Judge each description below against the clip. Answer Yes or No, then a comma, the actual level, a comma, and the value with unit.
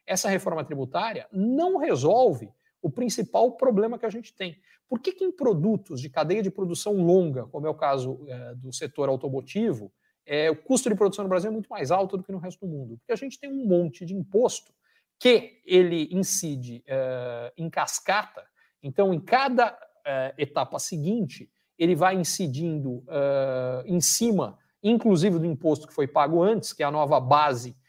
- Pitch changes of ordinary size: No, wide, 6.8 semitones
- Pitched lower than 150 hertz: No, medium, 175 Hz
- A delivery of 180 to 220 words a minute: Yes, fast, 185 wpm